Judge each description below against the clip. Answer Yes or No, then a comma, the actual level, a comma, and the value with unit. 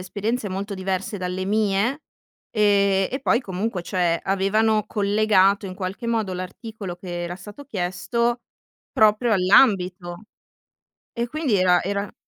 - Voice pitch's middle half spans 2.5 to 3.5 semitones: Yes, average, 2.9 semitones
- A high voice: Yes, high, 200 Hz